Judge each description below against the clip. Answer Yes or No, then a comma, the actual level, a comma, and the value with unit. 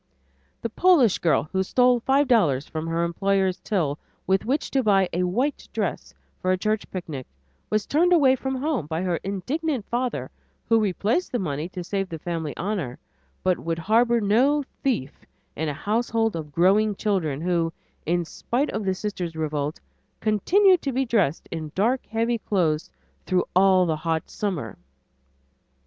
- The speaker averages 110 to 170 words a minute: Yes, average, 165 wpm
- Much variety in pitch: Yes, wide, 6.1 semitones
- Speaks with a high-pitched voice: Yes, high, 195 Hz